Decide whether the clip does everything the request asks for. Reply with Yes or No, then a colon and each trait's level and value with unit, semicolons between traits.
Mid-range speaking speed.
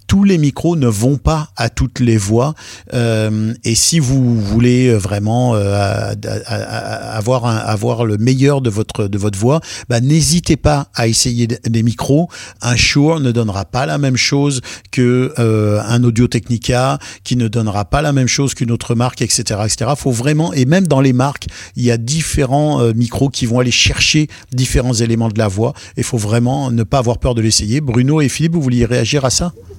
Yes: average, 200 wpm